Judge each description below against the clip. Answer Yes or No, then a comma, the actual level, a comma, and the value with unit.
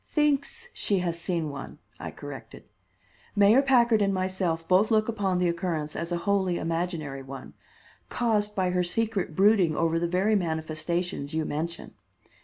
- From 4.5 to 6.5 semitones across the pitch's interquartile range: No, average, 3.9 semitones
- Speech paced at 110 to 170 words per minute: Yes, average, 155 wpm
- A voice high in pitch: No, medium, 180 Hz